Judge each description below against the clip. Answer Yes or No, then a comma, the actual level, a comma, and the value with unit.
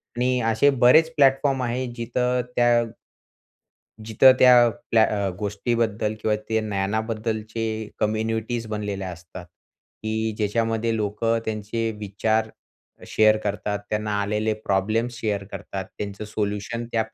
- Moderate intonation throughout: No, narrow, 2.1 semitones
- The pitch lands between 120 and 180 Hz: No, low, 110 Hz